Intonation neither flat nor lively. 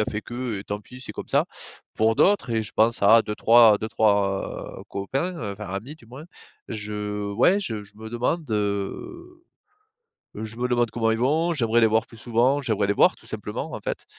Yes: average, 3.2 semitones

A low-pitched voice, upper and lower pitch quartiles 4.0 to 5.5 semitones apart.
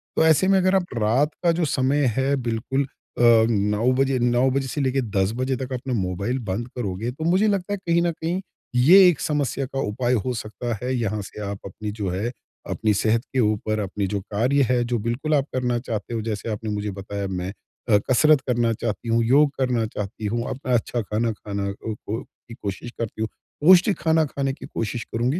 Yes: low, 120 Hz; average, 4.3 semitones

